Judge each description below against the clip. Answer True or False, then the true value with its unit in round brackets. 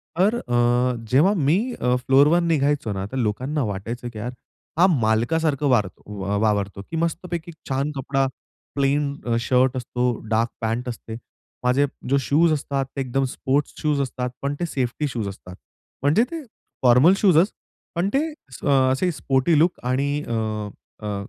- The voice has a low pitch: True (130 Hz)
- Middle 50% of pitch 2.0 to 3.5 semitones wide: False (4.2 semitones)